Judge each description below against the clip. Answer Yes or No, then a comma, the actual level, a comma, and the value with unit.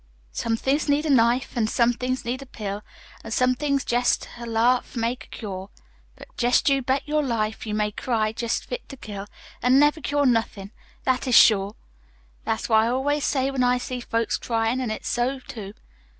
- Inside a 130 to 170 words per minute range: No, average, 200 wpm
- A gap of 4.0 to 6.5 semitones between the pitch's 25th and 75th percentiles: No, average, 3.0 semitones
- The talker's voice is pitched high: Yes, high, 245 Hz